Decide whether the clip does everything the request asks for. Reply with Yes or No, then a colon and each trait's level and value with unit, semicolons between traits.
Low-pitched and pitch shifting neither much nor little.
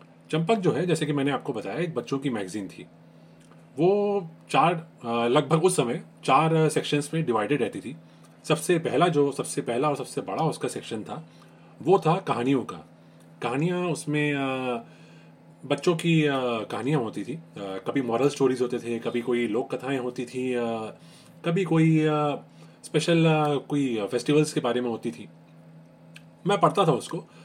No: low, 130 Hz; wide, 7.8 semitones